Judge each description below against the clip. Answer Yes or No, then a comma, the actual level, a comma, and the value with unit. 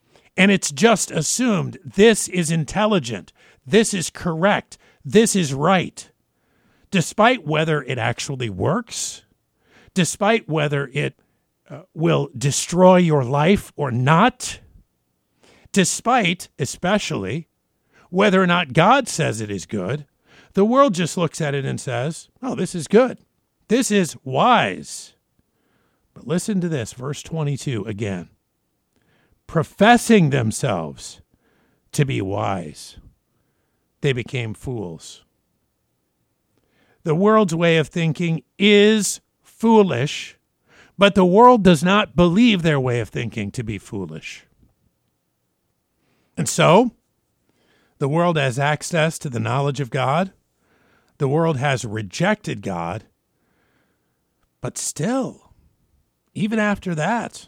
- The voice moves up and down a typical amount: No, wide, 6.3 semitones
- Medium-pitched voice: Yes, medium, 165 Hz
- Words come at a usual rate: No, slow, 115 wpm